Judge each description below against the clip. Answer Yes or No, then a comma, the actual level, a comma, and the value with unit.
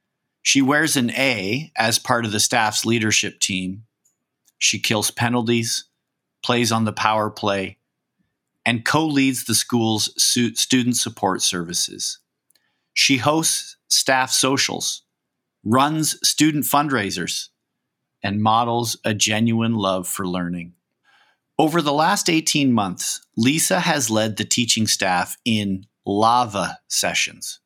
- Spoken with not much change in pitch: No, average, 4.2 semitones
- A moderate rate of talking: No, slow, 120 wpm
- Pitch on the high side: No, low, 115 Hz